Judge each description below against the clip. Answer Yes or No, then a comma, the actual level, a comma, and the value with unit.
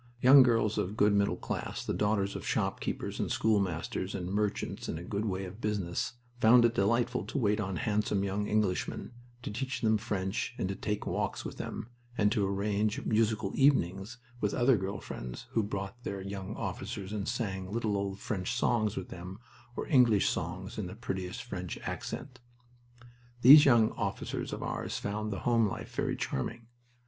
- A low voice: Yes, low, 105 Hz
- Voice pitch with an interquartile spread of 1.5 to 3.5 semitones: Yes, average, 2.8 semitones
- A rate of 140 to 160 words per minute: No, average, 175 wpm